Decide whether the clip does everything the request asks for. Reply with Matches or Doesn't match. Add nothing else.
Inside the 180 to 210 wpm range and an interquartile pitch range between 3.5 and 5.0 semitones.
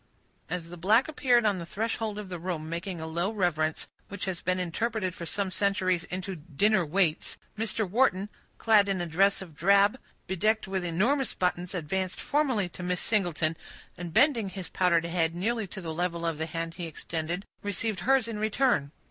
Matches